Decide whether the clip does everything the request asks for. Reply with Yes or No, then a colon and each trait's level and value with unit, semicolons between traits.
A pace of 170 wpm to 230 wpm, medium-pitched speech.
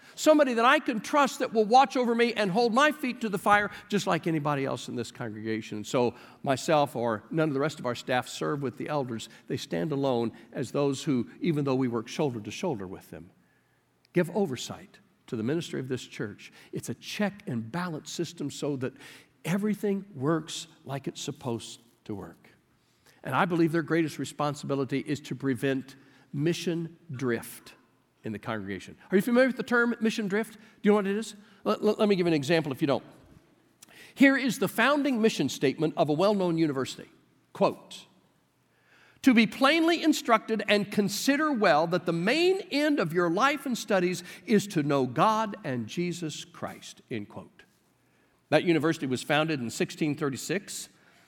Yes: average, 185 wpm; medium, 165 Hz